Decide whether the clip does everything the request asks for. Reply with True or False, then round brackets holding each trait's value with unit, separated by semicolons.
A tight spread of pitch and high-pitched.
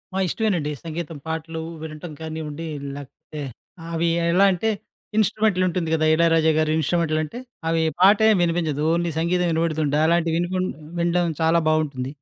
False (2.0 semitones; 165 Hz)